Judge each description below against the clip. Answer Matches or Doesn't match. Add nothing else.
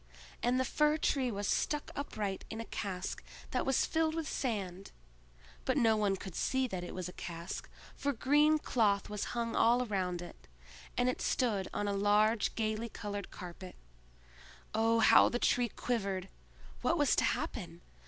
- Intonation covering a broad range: Doesn't match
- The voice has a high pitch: Matches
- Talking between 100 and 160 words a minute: Doesn't match